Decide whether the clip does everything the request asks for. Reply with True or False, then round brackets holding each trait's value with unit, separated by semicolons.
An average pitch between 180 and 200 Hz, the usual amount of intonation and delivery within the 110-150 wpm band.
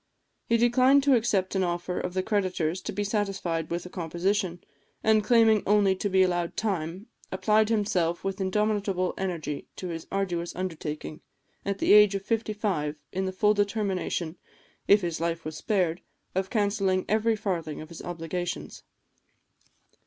False (190 Hz; 3.3 semitones; 160 wpm)